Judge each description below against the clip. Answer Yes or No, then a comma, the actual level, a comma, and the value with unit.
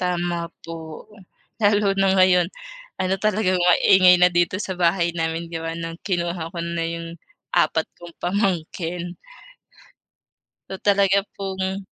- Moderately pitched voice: Yes, medium, 180 Hz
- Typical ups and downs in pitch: No, narrow, 2.2 semitones